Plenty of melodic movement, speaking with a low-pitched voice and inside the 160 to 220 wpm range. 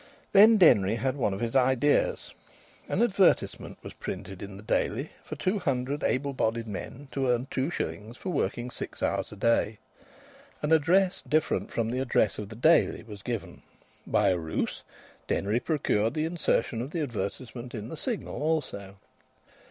Yes: wide, 6.3 semitones; low, 125 Hz; average, 165 wpm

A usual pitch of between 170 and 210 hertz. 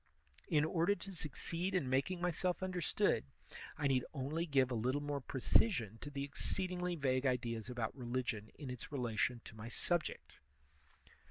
No: medium, 140 Hz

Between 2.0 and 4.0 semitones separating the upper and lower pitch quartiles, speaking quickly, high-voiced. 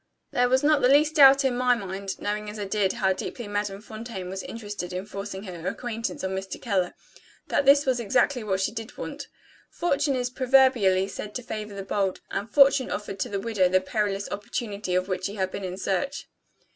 No: average, 4.4 semitones; fast, 210 wpm; high, 210 Hz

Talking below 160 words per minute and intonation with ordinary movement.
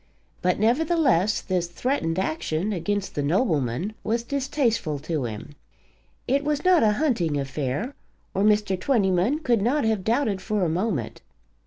No: average, 145 wpm; wide, 6.8 semitones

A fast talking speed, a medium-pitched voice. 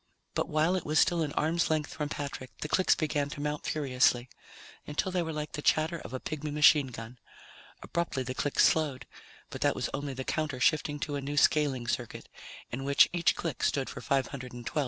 Yes: fast, 220 wpm; medium, 145 Hz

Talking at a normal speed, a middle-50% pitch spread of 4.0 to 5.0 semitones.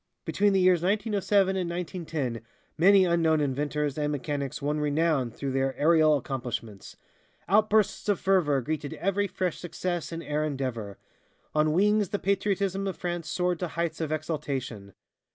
Yes: average, 150 wpm; average, 4.5 semitones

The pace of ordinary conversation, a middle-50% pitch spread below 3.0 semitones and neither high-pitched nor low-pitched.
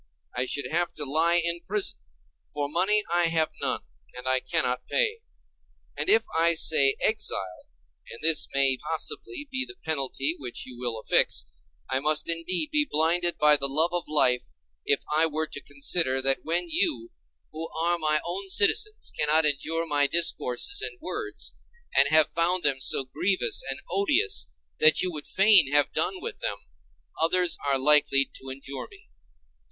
No: average, 170 wpm; average, 4.3 semitones; medium, 160 Hz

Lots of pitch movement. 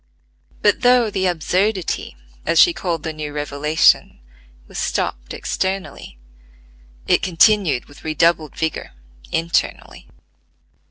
No: average, 4.1 semitones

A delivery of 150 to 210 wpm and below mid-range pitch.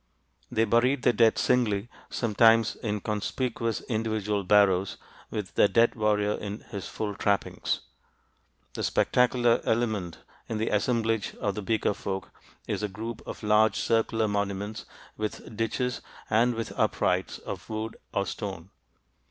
No: slow, 135 wpm; low, 110 Hz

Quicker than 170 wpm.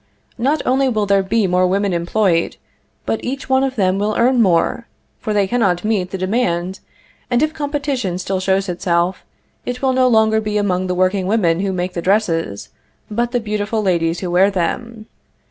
Yes: average, 180 wpm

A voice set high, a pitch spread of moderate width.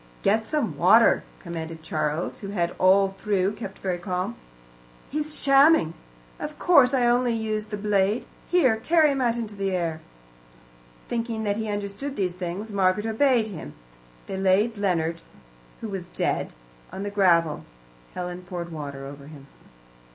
Yes: high, 200 Hz; average, 4.3 semitones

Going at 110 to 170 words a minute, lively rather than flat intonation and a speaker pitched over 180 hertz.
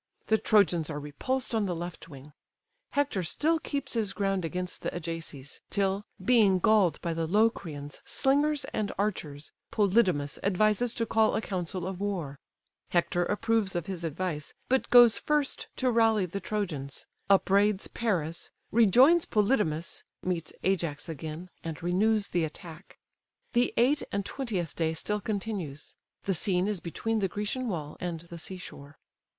No: average, 150 wpm; average, 4.8 semitones; high, 190 Hz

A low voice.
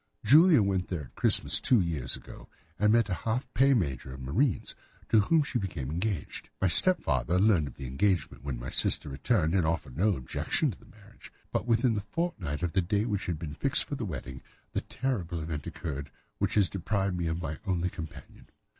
Yes: very low, 90 Hz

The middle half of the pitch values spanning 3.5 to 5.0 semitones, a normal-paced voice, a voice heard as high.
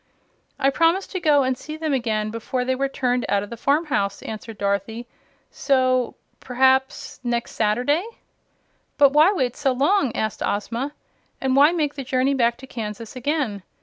Yes: average, 3.8 semitones; average, 170 wpm; very high, 260 Hz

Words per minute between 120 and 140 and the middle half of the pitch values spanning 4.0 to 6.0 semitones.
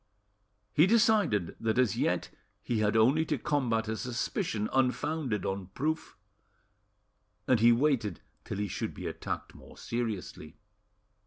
Yes: slow, 135 wpm; wide, 5.5 semitones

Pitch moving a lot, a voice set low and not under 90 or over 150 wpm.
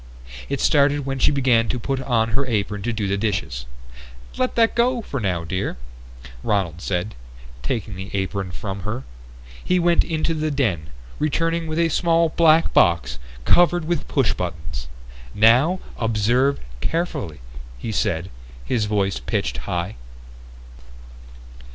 Yes: wide, 8.3 semitones; low, 115 Hz; average, 140 wpm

